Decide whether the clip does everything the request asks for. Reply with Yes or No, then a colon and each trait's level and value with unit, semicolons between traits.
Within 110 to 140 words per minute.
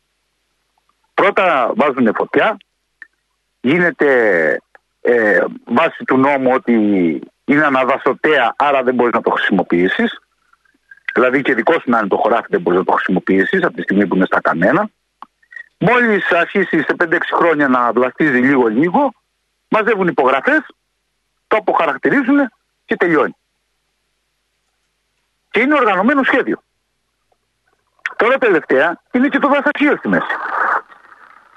Yes: average, 120 wpm